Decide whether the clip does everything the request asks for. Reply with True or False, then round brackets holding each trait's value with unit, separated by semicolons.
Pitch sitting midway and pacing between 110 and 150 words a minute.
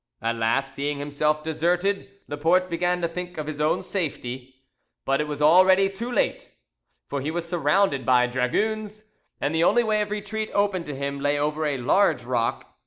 False (155 Hz; 180 wpm)